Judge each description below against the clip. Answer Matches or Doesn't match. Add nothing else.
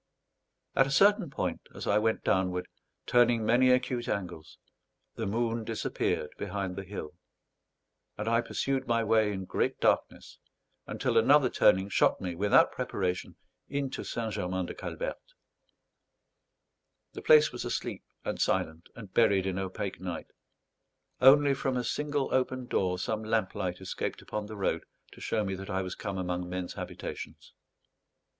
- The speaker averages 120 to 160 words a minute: Matches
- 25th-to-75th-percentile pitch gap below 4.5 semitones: Doesn't match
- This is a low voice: Matches